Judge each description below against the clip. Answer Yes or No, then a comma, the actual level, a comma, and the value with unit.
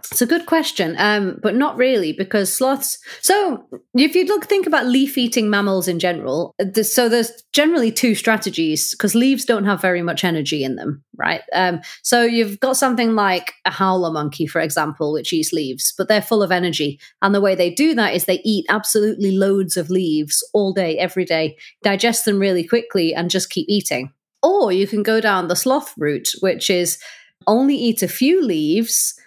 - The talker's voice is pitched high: Yes, high, 205 Hz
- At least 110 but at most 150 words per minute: No, average, 195 wpm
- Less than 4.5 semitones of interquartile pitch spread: No, wide, 5.4 semitones